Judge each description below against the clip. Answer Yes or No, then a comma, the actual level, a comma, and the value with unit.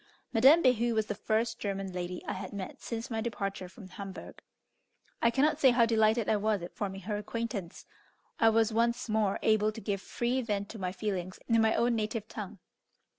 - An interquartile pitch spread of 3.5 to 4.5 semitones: No, average, 2.7 semitones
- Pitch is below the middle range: No, high, 215 Hz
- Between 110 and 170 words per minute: No, average, 195 wpm